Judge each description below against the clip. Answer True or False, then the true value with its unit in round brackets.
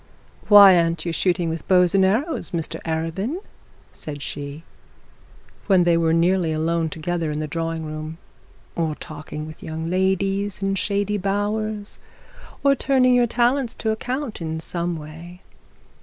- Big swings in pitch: False (4.0 semitones)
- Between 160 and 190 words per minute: False (145 wpm)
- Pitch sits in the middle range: True (175 Hz)